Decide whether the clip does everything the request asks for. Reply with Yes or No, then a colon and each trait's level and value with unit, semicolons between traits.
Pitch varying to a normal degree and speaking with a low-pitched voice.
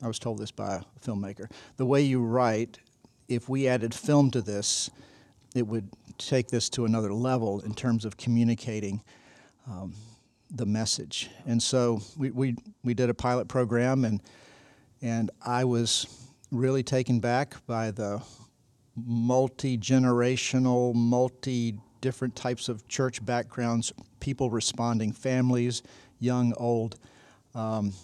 No: narrow, 2.3 semitones; low, 120 Hz